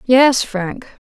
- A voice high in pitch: Yes, high, 235 Hz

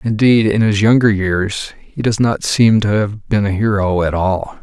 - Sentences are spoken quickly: Yes, fast, 210 wpm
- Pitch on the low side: Yes, low, 105 Hz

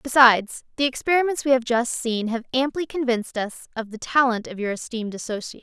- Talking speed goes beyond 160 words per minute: Yes, average, 190 wpm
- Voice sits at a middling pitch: No, high, 245 Hz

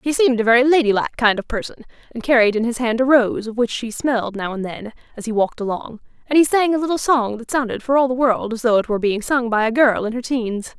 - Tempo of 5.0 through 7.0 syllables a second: Yes, 6.3 syllables/s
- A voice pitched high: Yes, high, 240 Hz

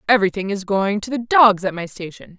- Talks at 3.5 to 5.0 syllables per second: No, 5.8 syllables/s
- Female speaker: Yes, female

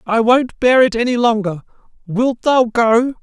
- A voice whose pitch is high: Yes, high, 235 Hz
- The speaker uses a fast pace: No, average, 170 wpm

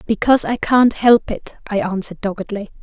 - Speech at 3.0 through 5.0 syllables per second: No, 5.7 syllables/s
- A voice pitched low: No, high, 215 Hz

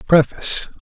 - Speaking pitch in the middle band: Yes, medium, 155 Hz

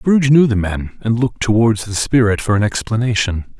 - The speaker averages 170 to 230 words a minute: Yes, average, 200 wpm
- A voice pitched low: Yes, low, 110 Hz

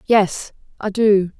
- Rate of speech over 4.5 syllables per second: No, 3.1 syllables/s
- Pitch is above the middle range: Yes, high, 200 Hz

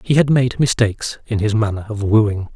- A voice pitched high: No, low, 110 Hz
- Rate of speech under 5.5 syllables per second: Yes, 5.2 syllables/s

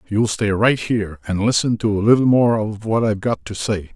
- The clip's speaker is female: No, male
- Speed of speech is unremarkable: No, fast, 245 wpm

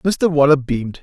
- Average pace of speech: Yes, average, 175 wpm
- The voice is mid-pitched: Yes, medium, 145 Hz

